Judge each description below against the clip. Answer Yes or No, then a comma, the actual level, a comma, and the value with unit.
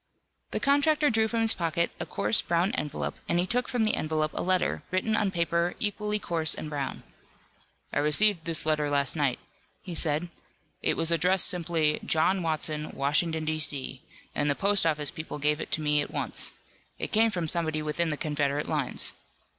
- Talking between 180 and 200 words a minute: Yes, average, 185 wpm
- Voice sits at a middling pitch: Yes, medium, 165 Hz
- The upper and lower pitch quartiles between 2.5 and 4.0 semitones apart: Yes, average, 3.7 semitones